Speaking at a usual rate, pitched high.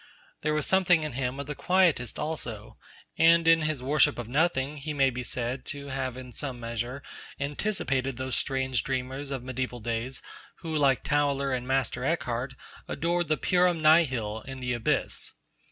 No: average, 170 wpm; low, 135 Hz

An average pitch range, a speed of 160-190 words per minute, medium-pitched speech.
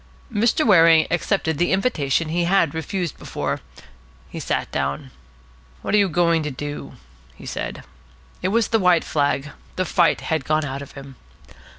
Yes: average, 4.4 semitones; average, 165 wpm; medium, 165 Hz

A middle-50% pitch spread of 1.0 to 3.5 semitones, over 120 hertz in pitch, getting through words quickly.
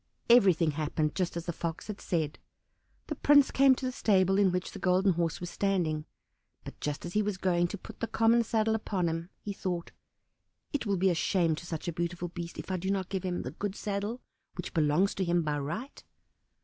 Yes: average, 3.2 semitones; medium, 185 Hz; fast, 220 wpm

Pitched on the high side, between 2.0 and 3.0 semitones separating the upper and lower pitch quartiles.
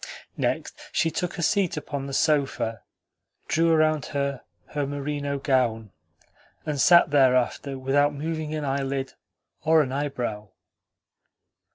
No: medium, 140 Hz; narrow, 2.5 semitones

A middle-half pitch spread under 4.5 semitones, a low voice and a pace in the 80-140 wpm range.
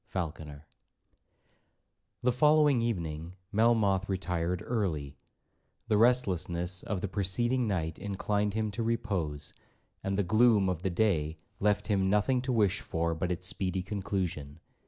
Yes: average, 4.1 semitones; very low, 95 Hz; slow, 135 wpm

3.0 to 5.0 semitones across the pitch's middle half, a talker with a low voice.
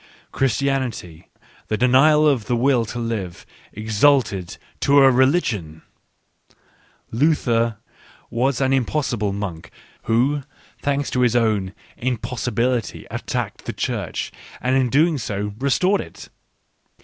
Yes: average, 4.0 semitones; low, 125 Hz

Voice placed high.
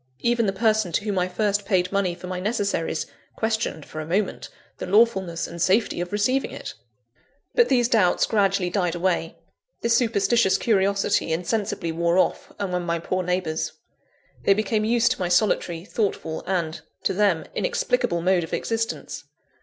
Yes: high, 195 Hz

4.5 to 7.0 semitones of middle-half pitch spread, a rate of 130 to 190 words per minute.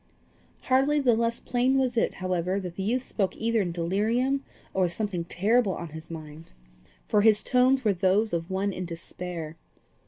Yes: wide, 5.4 semitones; average, 180 wpm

